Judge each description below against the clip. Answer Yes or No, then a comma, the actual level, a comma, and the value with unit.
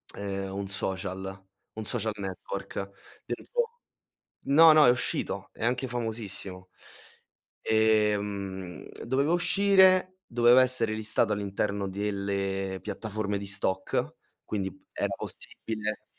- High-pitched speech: No, low, 105 Hz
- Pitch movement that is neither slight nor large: Yes, average, 3.6 semitones